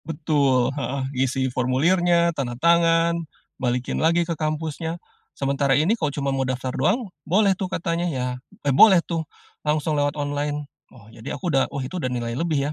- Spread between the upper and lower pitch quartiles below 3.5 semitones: No, average, 4.1 semitones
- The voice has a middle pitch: Yes, medium, 150 Hz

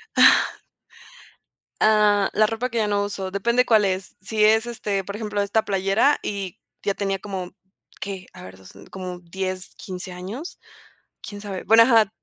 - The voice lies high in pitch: Yes, high, 200 Hz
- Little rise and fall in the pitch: Yes, narrow, 2.3 semitones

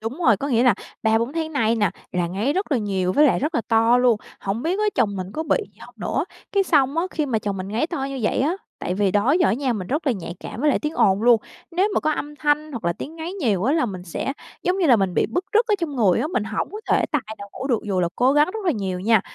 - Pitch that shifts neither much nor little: No, wide, 6.8 semitones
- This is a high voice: Yes, very high, 250 Hz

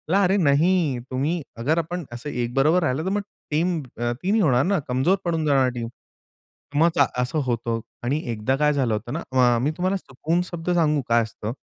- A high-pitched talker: No, medium, 145 Hz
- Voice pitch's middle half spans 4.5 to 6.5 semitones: Yes, wide, 5.6 semitones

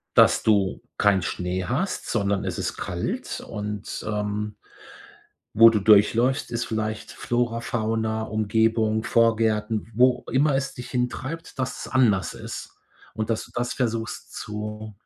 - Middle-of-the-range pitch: No, low, 110 Hz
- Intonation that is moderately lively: No, narrow, 2.3 semitones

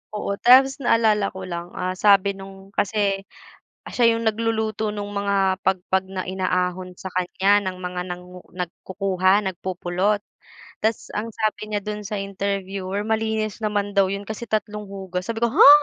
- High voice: Yes, high, 200 Hz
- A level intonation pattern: Yes, narrow, 2.3 semitones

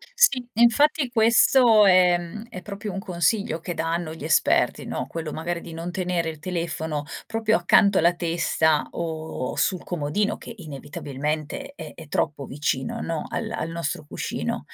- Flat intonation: No, average, 4.6 semitones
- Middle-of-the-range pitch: Yes, medium, 170 Hz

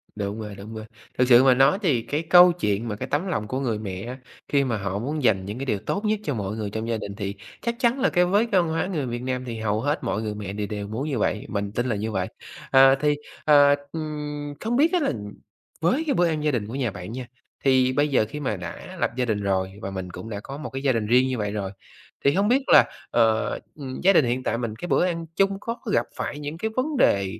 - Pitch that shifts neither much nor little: No, wide, 6.5 semitones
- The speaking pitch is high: No, low, 130 Hz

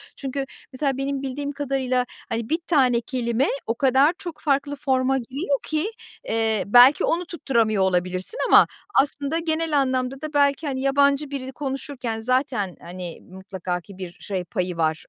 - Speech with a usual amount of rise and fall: Yes, average, 4.2 semitones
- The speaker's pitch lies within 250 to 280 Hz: Yes, very high, 265 Hz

